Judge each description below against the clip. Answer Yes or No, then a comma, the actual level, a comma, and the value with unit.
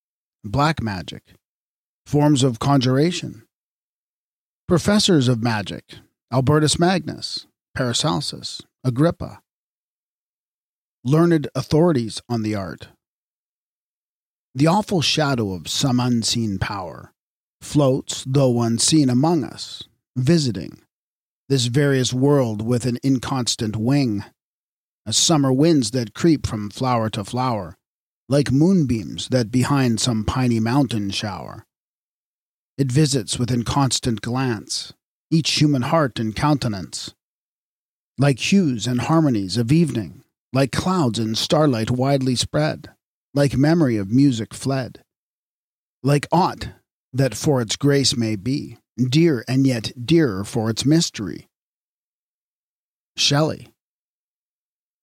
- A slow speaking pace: Yes, slow, 105 wpm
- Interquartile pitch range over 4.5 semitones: No, average, 4.2 semitones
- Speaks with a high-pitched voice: No, low, 130 Hz